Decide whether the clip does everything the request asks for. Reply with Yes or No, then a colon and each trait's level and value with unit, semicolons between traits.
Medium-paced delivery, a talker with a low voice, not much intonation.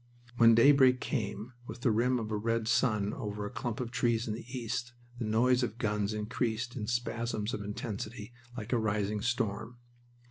Yes: average, 180 wpm; low, 115 Hz; narrow, 2.2 semitones